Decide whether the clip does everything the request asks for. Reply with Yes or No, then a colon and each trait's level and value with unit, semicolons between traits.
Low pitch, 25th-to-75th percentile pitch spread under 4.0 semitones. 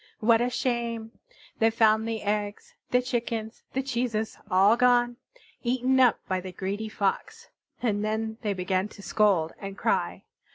No: high, 220 Hz; average, 2.8 semitones